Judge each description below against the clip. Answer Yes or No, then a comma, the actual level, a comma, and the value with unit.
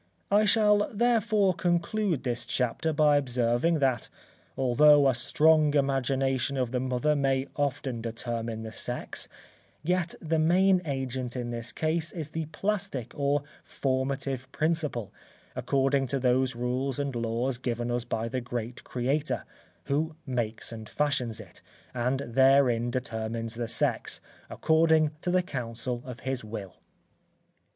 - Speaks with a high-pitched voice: No, low, 135 Hz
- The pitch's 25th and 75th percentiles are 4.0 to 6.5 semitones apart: Yes, average, 4.3 semitones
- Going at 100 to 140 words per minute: Yes, slow, 135 wpm